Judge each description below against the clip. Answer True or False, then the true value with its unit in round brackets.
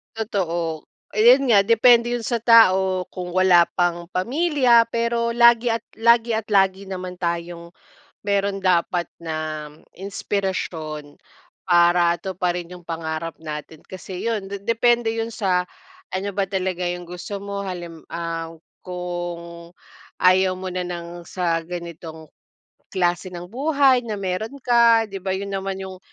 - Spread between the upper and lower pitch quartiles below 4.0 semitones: False (4.3 semitones)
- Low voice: False (185 Hz)